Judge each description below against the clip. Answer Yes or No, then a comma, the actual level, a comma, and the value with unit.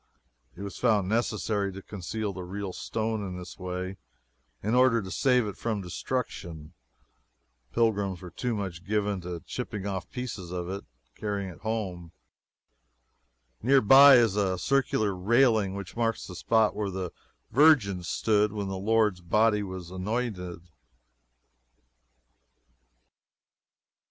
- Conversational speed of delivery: No, slow, 130 wpm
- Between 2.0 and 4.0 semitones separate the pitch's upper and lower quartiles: Yes, average, 3.4 semitones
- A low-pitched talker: Yes, low, 100 Hz